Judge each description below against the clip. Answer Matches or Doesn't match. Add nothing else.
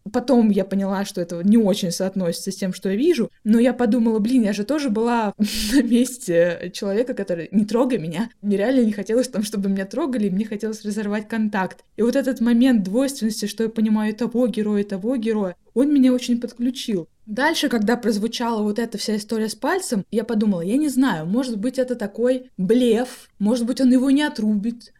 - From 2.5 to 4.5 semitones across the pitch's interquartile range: Matches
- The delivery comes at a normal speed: Doesn't match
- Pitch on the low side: Doesn't match